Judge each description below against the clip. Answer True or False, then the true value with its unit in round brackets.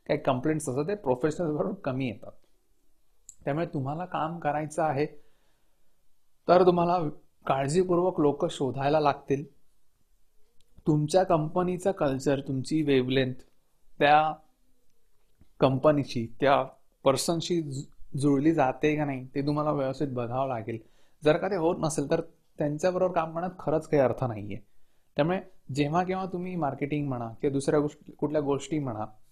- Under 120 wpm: False (125 wpm)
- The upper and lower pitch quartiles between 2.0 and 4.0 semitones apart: True (3.2 semitones)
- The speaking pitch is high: False (150 Hz)